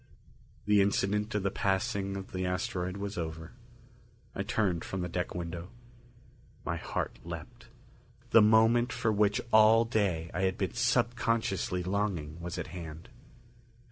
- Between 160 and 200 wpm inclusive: No, average, 140 wpm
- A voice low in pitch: Yes, low, 100 Hz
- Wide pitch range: No, average, 3.6 semitones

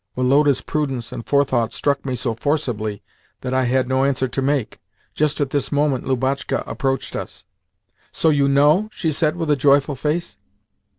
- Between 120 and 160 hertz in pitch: Yes, medium, 140 Hz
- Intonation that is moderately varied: No, narrow, 2.2 semitones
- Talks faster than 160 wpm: Yes, average, 170 wpm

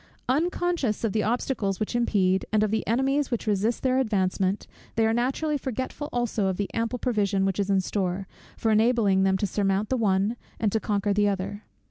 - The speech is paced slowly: No, average, 195 wpm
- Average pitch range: Yes, average, 3.6 semitones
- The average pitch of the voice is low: No, high, 215 Hz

